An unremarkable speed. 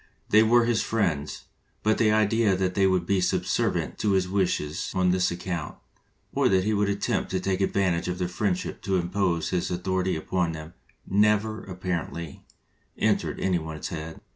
Yes: average, 180 wpm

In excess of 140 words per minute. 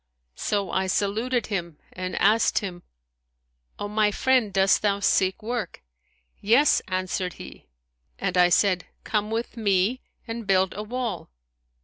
No: slow, 135 wpm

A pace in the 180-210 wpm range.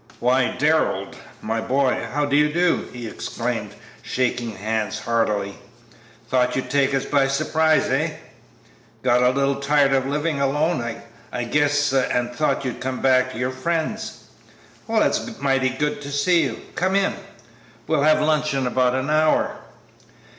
No: average, 155 wpm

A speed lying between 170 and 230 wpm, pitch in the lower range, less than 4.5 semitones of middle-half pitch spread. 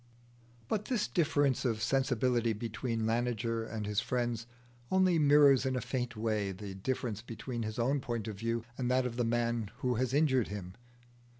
Yes: average, 175 wpm; low, 120 Hz; average, 2.8 semitones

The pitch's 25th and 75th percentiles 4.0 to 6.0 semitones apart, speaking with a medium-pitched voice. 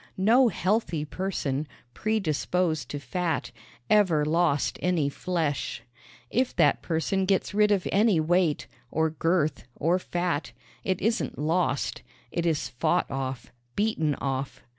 Yes: average, 4.3 semitones; medium, 170 Hz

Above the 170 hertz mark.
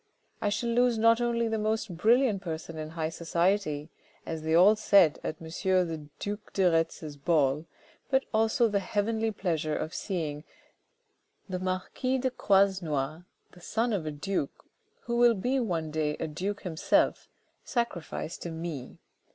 Yes: medium, 185 Hz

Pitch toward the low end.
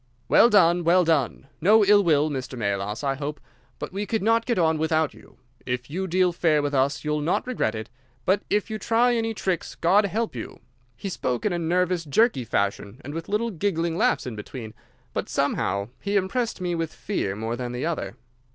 No: medium, 165 Hz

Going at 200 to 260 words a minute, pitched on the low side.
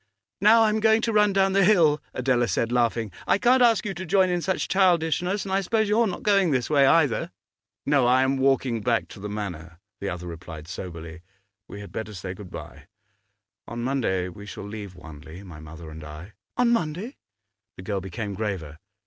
Yes: fast, 205 wpm; low, 120 Hz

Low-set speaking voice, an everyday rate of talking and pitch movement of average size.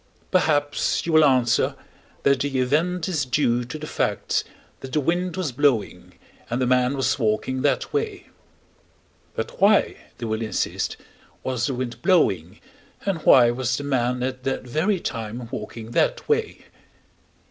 Yes: low, 130 Hz; average, 155 wpm; average, 4.6 semitones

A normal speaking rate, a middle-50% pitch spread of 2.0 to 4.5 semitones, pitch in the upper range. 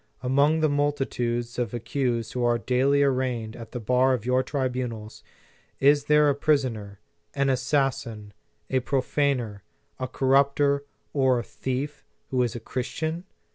No: average, 145 wpm; average, 2.8 semitones; low, 130 Hz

